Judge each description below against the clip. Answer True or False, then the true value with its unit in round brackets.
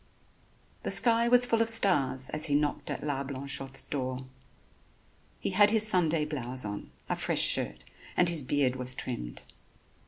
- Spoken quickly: False (160 wpm)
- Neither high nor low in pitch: True (145 Hz)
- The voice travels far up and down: True (6.3 semitones)